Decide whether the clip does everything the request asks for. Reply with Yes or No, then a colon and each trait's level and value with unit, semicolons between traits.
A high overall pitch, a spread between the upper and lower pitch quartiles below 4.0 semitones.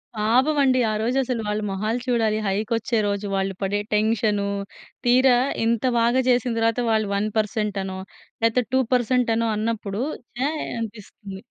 Yes: high, 225 Hz; average, 2.7 semitones